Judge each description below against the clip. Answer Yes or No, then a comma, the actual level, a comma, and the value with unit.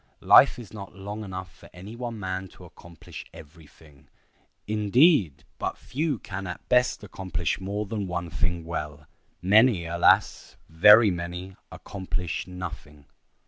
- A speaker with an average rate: No, slow, 130 wpm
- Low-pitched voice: Yes, very low, 95 Hz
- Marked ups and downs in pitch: No, average, 3.5 semitones